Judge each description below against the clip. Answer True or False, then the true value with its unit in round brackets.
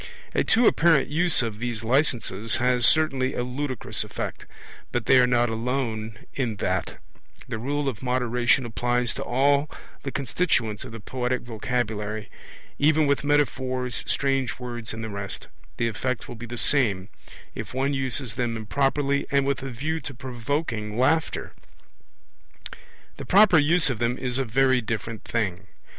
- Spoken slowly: False (155 wpm)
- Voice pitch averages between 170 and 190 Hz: False (125 Hz)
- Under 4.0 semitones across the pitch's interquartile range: True (3.4 semitones)